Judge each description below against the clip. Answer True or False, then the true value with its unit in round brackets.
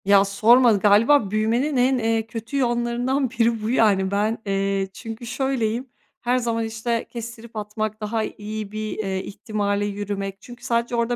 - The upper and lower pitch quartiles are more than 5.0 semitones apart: False (2.5 semitones)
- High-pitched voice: True (225 Hz)